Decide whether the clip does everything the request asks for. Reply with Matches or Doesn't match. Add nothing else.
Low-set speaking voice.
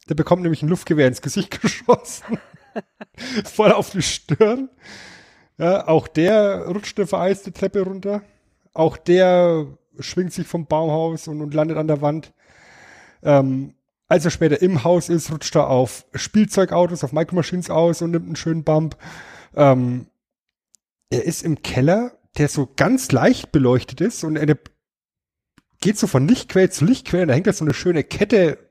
Doesn't match